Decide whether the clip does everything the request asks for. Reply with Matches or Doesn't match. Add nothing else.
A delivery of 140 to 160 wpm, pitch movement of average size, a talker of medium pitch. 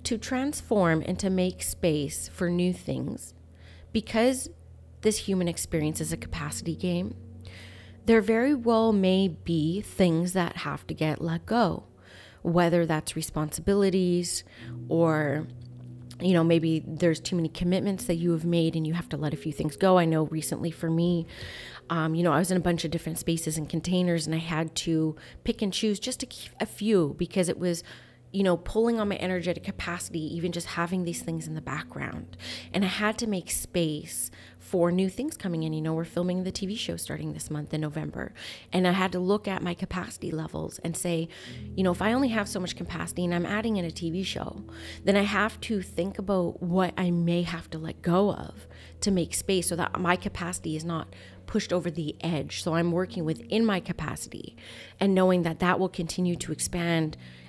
Doesn't match